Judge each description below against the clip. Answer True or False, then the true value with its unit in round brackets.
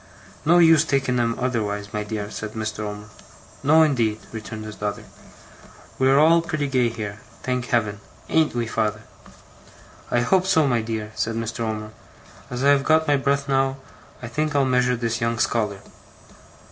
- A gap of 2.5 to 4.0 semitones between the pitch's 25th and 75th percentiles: False (4.4 semitones)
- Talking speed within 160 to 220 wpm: True (170 wpm)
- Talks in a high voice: False (120 Hz)